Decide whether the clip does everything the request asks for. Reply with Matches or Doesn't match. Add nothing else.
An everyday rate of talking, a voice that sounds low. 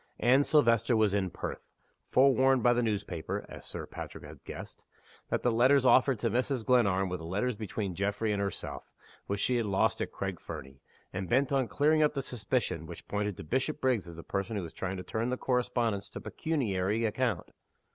Matches